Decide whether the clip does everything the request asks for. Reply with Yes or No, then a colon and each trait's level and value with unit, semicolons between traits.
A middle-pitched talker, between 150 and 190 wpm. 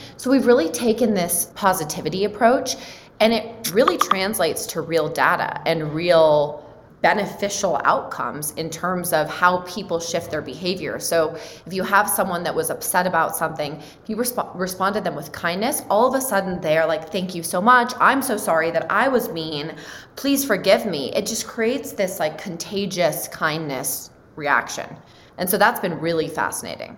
Yes: medium, 180 Hz; average, 175 wpm